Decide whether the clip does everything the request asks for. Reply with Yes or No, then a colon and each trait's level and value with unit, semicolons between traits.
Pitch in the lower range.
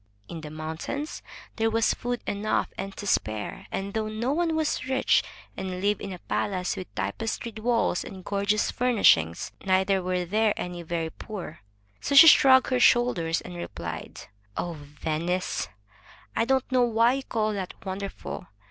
No: high, 200 Hz